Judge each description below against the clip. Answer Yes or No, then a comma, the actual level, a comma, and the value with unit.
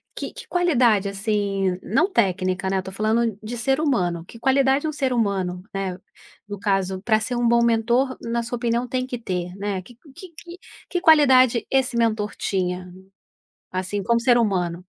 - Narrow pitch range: No, average, 4.7 semitones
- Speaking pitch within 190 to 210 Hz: No, high, 225 Hz